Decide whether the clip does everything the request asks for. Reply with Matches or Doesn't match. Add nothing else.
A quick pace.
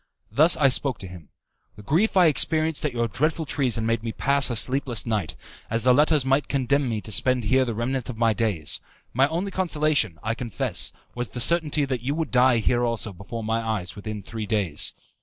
Matches